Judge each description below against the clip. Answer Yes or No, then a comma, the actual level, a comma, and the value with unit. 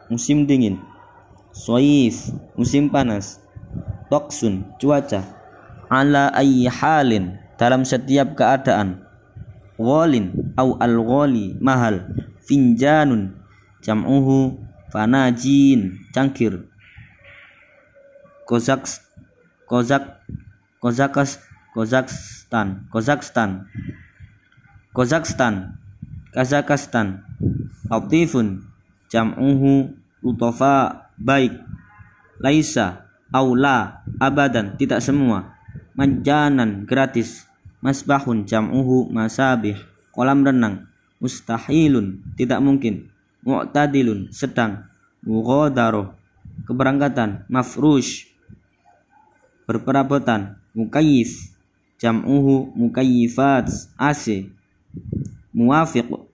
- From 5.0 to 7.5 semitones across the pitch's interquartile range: No, average, 4.5 semitones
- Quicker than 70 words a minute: No, slow, 65 wpm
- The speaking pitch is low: Yes, low, 120 Hz